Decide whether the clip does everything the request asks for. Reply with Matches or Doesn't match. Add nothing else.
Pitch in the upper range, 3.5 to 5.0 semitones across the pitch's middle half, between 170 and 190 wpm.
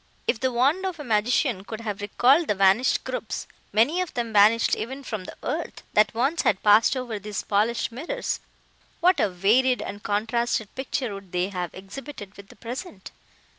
Matches